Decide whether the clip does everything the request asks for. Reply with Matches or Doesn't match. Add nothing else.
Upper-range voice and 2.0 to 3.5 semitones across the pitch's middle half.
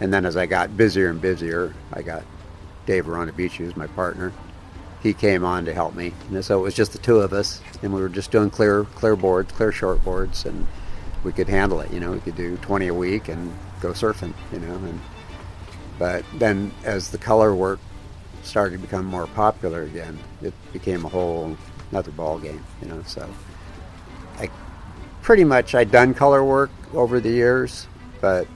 Doesn't match